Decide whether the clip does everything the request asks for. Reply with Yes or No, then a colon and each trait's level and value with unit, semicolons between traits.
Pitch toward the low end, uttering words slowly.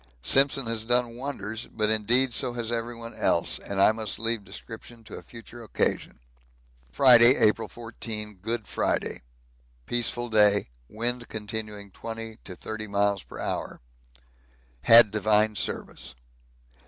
Yes: low, 115 Hz; slow, 130 wpm